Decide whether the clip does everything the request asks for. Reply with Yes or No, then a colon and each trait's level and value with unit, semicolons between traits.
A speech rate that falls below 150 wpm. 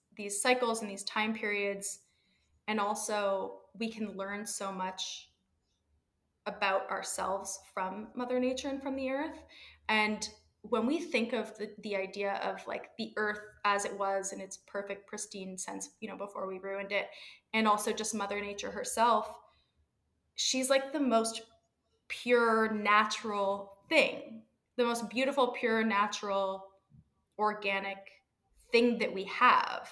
Yes: average, 140 wpm